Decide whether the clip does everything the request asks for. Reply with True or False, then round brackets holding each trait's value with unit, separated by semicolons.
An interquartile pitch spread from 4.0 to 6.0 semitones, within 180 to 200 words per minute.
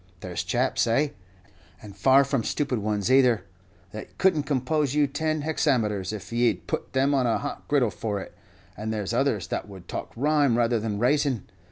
True (5.1 semitones; 185 wpm)